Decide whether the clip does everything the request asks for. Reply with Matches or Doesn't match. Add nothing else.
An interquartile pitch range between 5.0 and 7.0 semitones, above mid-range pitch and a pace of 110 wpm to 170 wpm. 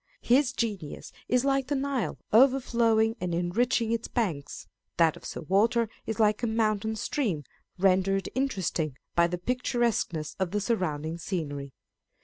Matches